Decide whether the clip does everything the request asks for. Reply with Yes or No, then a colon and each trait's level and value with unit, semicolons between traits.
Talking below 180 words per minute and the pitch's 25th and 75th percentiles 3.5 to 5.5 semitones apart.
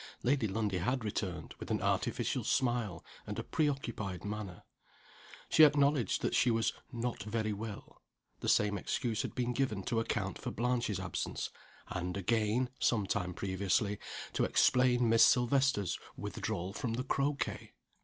Yes: average, 145 wpm; average, 3.8 semitones